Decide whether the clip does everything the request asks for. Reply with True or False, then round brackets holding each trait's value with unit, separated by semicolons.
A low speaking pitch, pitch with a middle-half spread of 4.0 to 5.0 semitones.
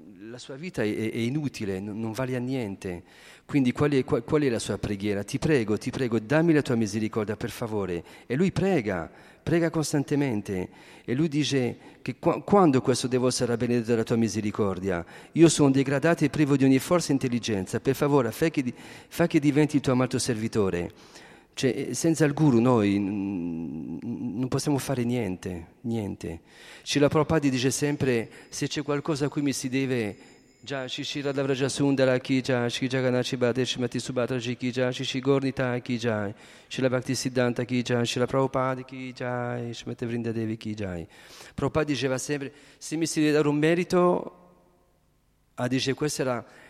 False (130 Hz; 3.5 semitones)